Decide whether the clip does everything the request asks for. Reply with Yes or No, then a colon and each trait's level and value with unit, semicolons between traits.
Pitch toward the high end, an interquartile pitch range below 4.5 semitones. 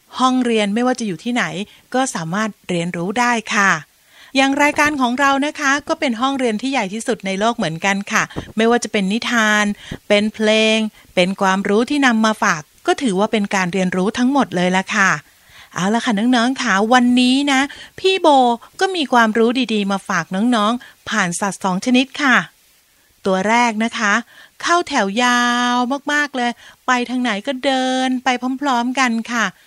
Yes: high, 235 Hz; average, 3.9 semitones